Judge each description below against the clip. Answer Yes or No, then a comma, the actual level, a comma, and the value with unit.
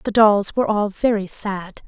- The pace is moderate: Yes, average, 190 wpm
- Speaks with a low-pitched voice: No, high, 205 Hz